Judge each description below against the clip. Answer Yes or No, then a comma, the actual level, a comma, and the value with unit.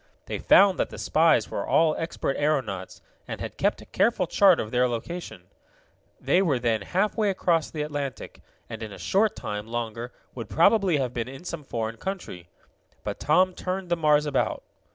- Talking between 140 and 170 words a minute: No, average, 180 wpm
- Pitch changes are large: Yes, wide, 7.3 semitones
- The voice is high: No, medium, 150 Hz